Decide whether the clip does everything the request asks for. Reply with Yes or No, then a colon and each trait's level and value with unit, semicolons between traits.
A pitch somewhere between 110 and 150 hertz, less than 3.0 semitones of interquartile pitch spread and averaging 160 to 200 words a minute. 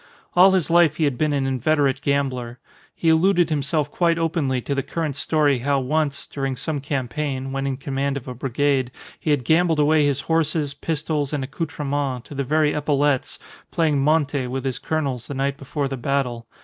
Yes: medium, 140 Hz; narrow, 2.5 semitones; average, 190 wpm